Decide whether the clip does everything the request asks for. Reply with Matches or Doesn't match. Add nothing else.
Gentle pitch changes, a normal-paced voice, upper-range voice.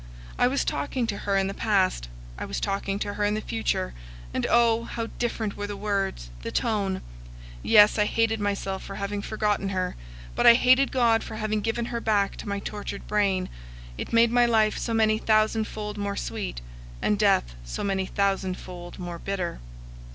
Matches